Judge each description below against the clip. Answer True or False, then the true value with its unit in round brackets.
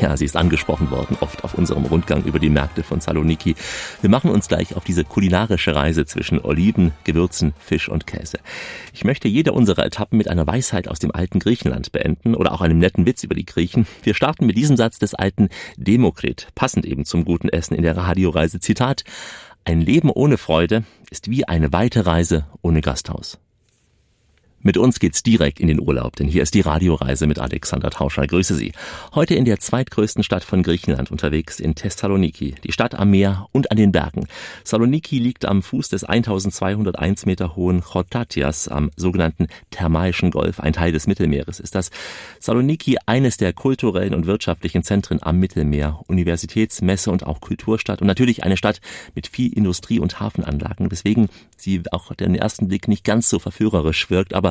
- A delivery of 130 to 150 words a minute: False (185 wpm)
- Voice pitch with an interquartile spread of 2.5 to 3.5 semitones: False (4.4 semitones)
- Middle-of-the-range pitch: False (90 Hz)